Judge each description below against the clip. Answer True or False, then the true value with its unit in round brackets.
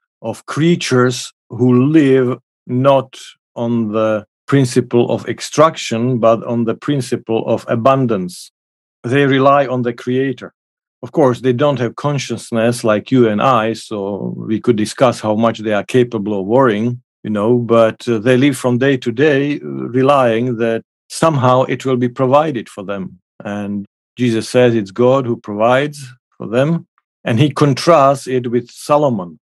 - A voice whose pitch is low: True (125 Hz)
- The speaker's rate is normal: True (155 wpm)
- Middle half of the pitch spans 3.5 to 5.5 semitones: False (3.1 semitones)